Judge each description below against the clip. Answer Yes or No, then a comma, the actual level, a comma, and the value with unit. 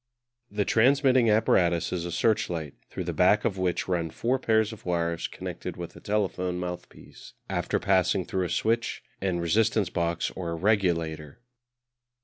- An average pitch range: Yes, average, 4.0 semitones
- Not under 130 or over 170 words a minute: Yes, average, 150 wpm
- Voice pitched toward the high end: No, very low, 95 Hz